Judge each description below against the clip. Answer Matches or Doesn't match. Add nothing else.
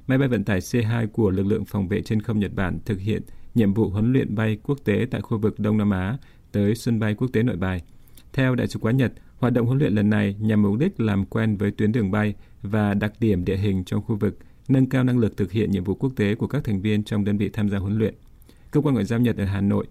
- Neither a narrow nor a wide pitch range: Doesn't match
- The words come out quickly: Matches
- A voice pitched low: Matches